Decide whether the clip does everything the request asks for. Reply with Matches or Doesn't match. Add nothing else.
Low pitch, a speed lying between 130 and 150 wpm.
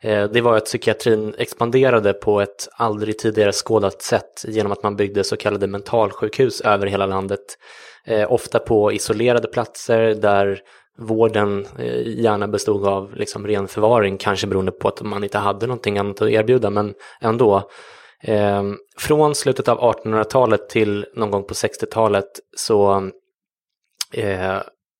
Matches